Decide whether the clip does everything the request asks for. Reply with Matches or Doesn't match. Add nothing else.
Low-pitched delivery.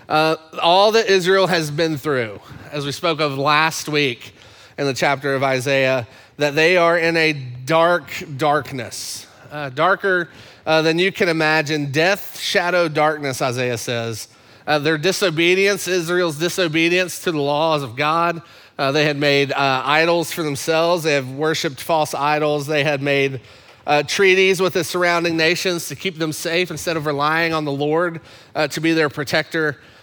Doesn't match